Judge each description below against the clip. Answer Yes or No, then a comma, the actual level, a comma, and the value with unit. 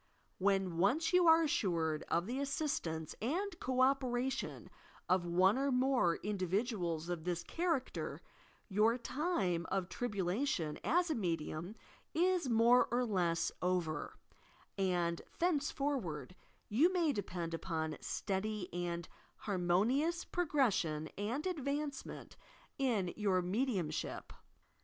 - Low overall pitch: No, high, 210 Hz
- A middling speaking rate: No, slow, 115 wpm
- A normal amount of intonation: No, wide, 7.8 semitones